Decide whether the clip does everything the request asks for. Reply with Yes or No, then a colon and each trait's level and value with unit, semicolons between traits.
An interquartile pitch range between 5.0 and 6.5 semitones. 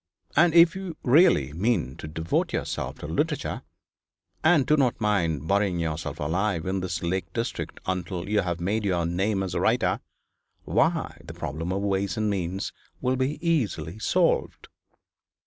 Yes: average, 5.3 semitones